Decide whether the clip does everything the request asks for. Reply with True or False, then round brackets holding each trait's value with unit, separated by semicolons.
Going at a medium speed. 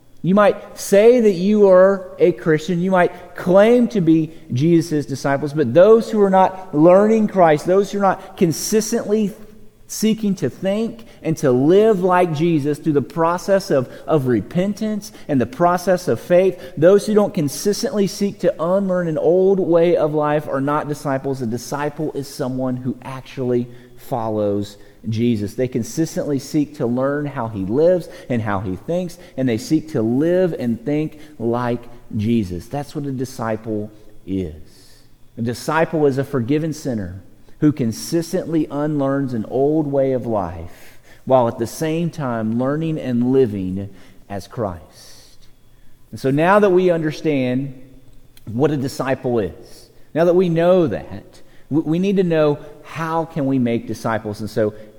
True (160 wpm)